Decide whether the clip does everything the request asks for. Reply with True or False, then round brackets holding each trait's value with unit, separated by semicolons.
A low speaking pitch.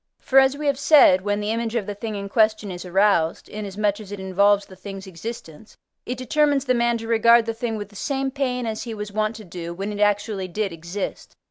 False (210 Hz)